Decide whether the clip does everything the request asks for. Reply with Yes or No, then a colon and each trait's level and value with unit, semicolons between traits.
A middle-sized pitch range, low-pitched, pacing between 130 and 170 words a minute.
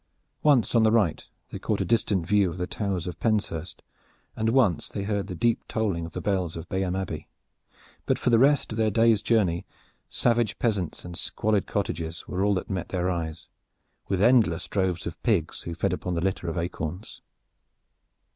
No: average, 4.2 semitones; very low, 95 Hz; average, 190 wpm